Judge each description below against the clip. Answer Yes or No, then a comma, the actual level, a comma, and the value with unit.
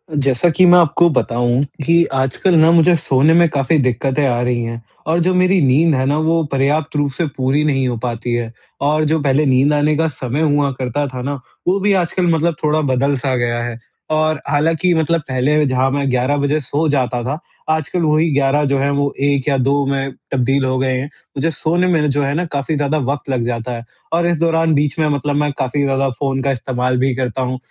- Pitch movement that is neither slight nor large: Yes, average, 3.2 semitones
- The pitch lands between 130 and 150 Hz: Yes, medium, 140 Hz